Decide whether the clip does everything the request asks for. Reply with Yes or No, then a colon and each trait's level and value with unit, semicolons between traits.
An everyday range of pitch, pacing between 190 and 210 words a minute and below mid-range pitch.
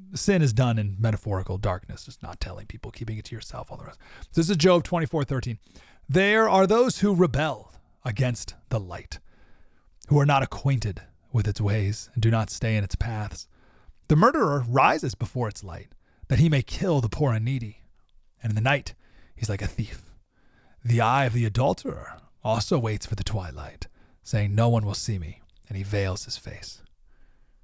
Yes: average, 4.9 semitones; average, 195 wpm; low, 115 Hz